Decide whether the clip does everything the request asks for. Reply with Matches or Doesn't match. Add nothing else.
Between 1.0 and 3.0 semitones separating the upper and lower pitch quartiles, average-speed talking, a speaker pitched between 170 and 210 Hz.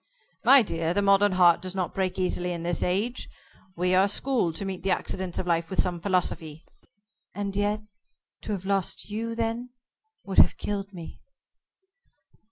Matches